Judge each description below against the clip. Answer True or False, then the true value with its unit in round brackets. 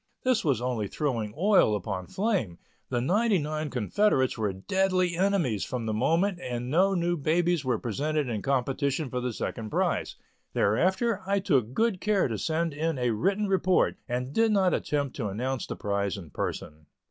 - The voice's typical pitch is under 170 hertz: True (140 Hz)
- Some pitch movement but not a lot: False (7.9 semitones)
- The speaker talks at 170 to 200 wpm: True (175 wpm)